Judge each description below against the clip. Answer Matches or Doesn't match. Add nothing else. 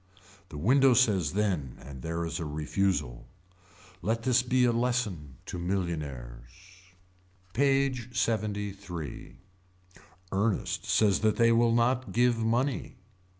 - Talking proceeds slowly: Matches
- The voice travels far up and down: Matches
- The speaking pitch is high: Doesn't match